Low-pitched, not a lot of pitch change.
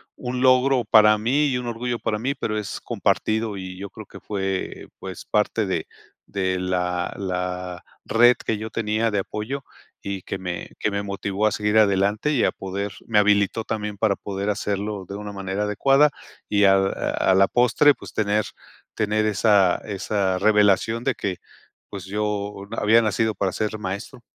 Yes: low, 105 Hz; narrow, 2.2 semitones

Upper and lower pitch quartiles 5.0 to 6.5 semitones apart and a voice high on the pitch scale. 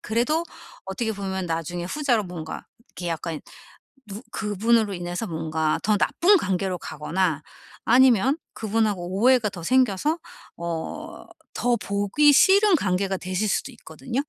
Yes: wide, 5.4 semitones; high, 200 Hz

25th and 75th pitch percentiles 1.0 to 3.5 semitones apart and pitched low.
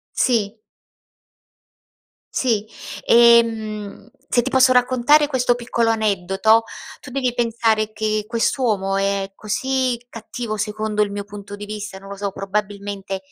No: average, 2.8 semitones; high, 215 Hz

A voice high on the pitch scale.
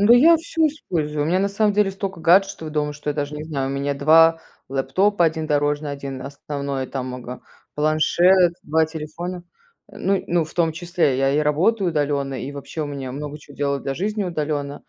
No: medium, 155 Hz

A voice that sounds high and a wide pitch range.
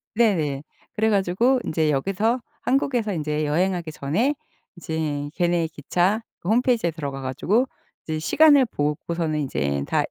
No: medium, 170 Hz; wide, 6.6 semitones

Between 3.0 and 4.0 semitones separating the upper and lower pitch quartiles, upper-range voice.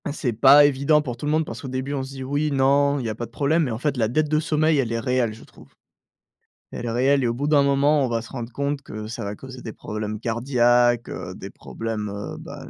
No: average, 3.5 semitones; low, 130 Hz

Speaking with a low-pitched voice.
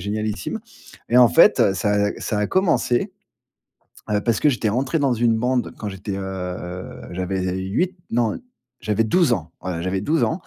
Yes: low, 105 Hz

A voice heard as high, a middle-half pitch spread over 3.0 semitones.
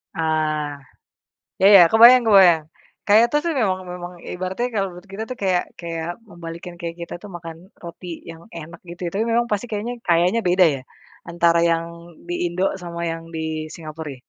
No: medium, 175 Hz; average, 3.4 semitones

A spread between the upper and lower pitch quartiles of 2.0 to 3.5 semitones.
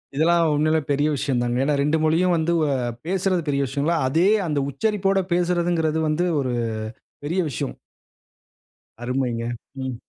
No: average, 4.0 semitones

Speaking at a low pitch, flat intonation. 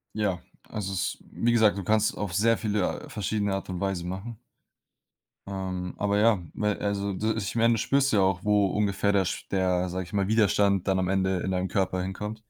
Yes: low, 100 Hz; narrow, 2.1 semitones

